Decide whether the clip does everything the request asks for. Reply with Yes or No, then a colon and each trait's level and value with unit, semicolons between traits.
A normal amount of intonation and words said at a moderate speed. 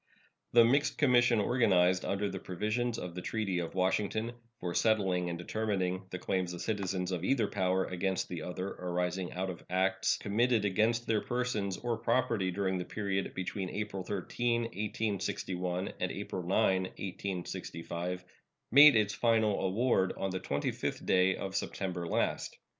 Yes: average, 3.3 semitones; average, 155 wpm